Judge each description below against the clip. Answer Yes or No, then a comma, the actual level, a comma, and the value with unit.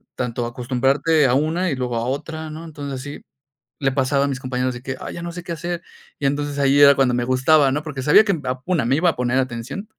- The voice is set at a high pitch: No, medium, 140 Hz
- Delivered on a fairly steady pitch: No, average, 3.6 semitones